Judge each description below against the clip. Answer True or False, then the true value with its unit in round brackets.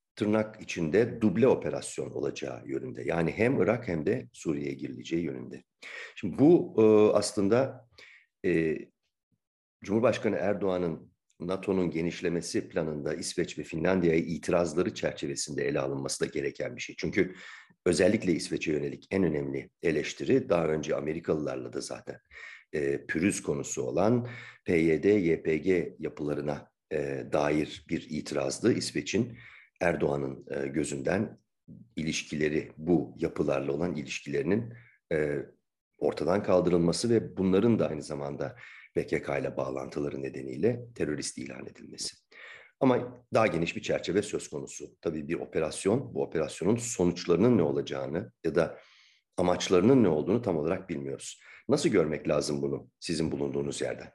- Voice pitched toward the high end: False (80 Hz)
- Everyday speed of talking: True (120 wpm)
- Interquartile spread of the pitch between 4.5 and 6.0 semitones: True (5.4 semitones)